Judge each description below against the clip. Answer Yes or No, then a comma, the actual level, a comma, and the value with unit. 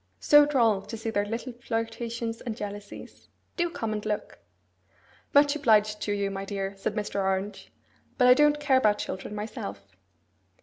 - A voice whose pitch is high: Yes, high, 215 Hz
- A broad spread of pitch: No, average, 3.2 semitones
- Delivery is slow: No, average, 165 wpm